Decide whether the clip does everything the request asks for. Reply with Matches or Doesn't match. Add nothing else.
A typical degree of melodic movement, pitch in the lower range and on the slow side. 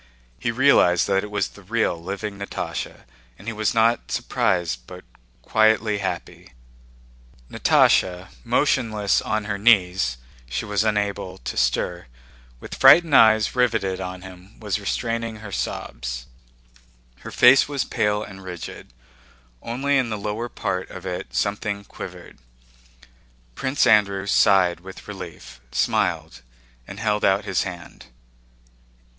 Matches